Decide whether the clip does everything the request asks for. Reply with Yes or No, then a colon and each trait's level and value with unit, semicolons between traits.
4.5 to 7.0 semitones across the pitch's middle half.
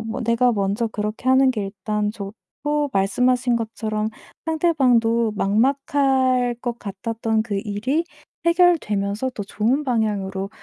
No: average, 3.7 semitones